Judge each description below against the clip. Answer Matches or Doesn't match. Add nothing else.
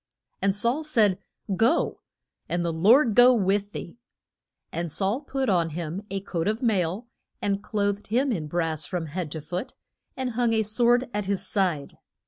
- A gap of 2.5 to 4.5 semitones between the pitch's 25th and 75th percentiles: Doesn't match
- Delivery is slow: Doesn't match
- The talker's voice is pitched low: Doesn't match